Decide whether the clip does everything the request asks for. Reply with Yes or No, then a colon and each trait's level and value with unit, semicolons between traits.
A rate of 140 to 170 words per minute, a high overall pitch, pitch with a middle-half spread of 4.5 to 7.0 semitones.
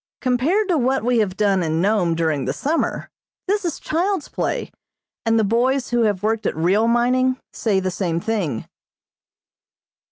Yes: average, 165 wpm; high, 225 Hz; wide, 5.5 semitones